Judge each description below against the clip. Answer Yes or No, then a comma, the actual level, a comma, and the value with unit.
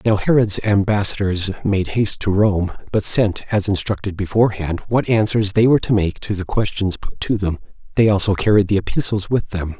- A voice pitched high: No, low, 100 Hz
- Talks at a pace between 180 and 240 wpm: Yes, average, 190 wpm